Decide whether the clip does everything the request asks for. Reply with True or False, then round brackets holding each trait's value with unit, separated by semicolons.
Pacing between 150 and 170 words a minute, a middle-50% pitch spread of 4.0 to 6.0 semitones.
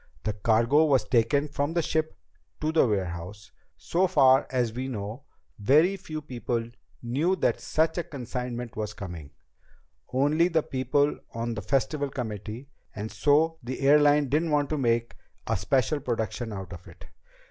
True (160 wpm; 4.8 semitones)